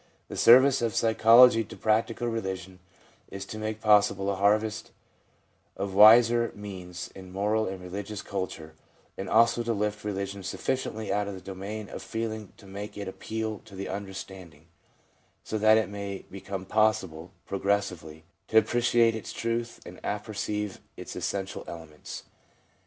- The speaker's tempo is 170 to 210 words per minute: No, average, 150 wpm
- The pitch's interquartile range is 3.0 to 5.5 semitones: No, narrow, 2.4 semitones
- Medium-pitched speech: No, low, 105 Hz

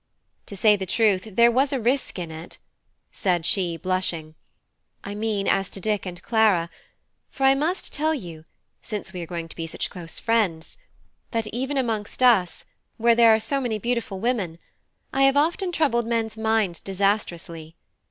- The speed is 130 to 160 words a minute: No, average, 170 wpm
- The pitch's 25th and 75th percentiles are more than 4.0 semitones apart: Yes, average, 4.8 semitones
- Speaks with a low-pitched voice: No, high, 215 Hz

